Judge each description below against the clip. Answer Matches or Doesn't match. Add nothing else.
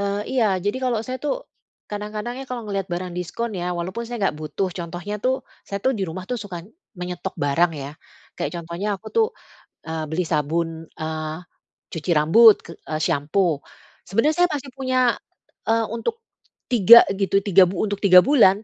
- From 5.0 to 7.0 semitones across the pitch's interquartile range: Matches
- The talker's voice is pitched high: Matches